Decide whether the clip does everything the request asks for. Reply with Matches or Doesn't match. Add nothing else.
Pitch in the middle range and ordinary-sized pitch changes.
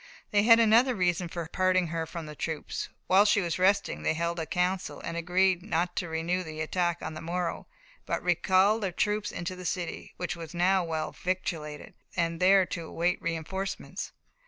Doesn't match